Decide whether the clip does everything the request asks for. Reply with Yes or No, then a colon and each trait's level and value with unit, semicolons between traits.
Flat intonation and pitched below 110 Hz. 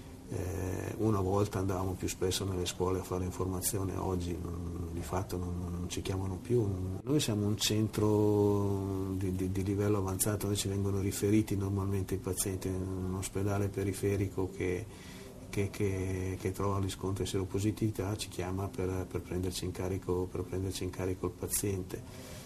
Yes: narrow, 1.6 semitones; very low, 95 Hz